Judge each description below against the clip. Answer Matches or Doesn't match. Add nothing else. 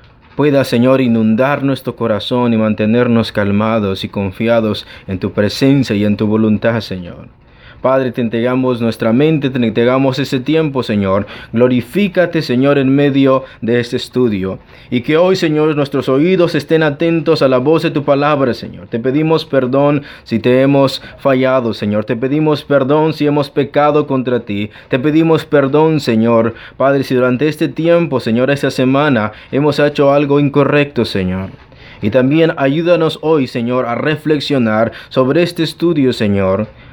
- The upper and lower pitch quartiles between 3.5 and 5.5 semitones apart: Matches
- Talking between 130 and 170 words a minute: Matches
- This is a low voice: Matches